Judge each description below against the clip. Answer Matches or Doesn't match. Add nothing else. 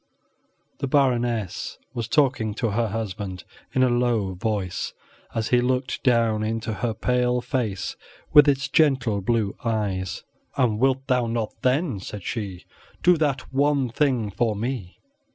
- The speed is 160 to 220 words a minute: Doesn't match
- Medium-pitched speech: Doesn't match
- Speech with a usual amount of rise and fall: Matches